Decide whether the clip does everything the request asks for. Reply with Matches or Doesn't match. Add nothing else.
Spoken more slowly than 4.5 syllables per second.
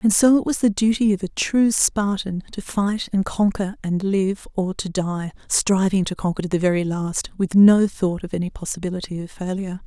Doesn't match